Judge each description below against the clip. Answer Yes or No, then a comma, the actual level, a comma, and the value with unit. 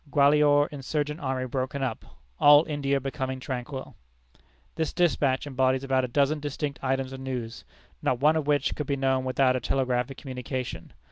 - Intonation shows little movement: Yes, narrow, 2.0 semitones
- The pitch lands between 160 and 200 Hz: No, low, 135 Hz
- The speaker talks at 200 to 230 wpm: No, average, 160 wpm